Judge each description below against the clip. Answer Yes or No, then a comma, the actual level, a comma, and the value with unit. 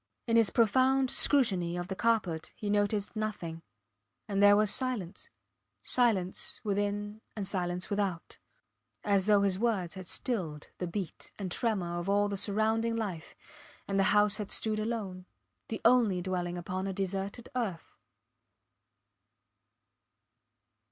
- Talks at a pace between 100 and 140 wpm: Yes, slow, 135 wpm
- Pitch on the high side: Yes, high, 205 Hz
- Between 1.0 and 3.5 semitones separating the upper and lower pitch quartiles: Yes, average, 3.1 semitones